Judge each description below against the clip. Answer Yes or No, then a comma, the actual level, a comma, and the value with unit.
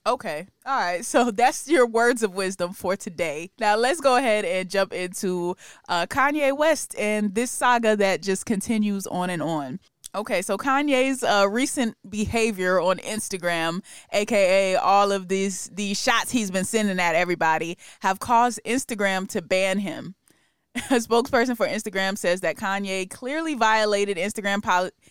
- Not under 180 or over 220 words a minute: No, average, 160 wpm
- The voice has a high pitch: Yes, high, 205 Hz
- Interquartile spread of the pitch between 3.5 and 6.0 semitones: Yes, average, 4.2 semitones